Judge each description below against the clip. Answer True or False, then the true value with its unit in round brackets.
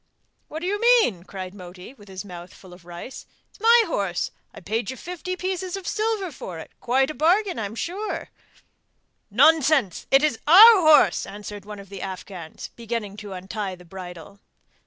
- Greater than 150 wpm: True (180 wpm)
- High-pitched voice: True (220 Hz)